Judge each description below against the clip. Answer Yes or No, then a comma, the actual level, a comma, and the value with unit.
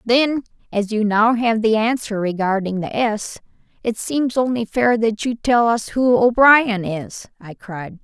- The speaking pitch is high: Yes, high, 225 Hz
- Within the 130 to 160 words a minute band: No, average, 170 wpm